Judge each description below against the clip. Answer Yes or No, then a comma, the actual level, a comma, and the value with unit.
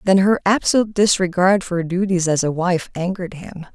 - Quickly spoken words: No, average, 190 wpm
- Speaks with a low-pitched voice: No, medium, 185 Hz